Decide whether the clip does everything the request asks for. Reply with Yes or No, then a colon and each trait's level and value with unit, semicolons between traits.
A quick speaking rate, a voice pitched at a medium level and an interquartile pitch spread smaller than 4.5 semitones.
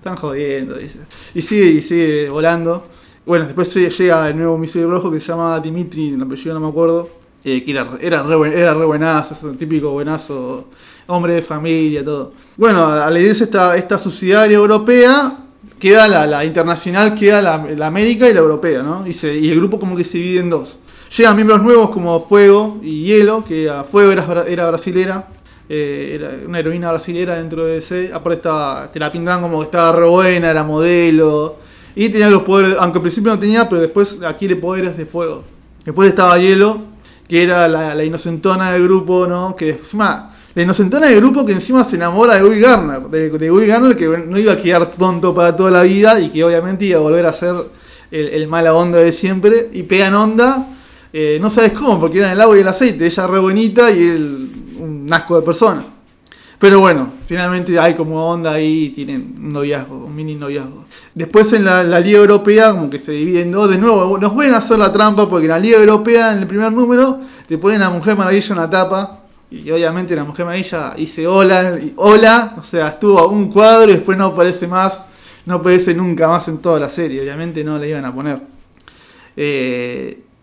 Yes: fast, 205 wpm; medium, 175 Hz; average, 4.1 semitones